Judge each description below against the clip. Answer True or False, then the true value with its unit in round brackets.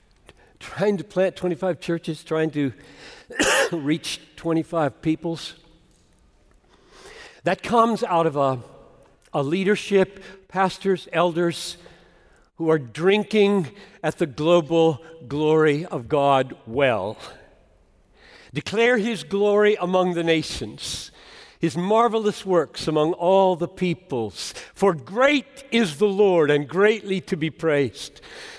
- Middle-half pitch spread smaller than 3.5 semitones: False (4.1 semitones)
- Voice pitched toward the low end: False (175 Hz)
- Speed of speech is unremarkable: False (110 wpm)